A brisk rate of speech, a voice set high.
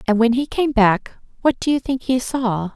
Yes: fast, 240 wpm; high, 245 Hz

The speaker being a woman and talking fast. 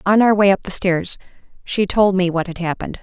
Yes: female; fast, 240 wpm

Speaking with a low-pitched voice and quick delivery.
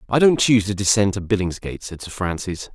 Yes: low, 100 Hz; fast, 220 wpm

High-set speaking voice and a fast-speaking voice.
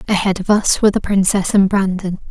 Yes: high, 195 Hz; fast, 210 wpm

